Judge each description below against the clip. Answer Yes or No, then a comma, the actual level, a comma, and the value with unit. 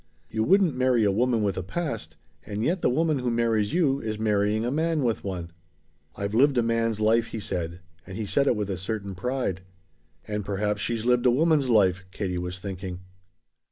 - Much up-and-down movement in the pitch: No, average, 4.1 semitones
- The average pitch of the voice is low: Yes, low, 110 Hz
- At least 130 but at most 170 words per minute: No, average, 200 wpm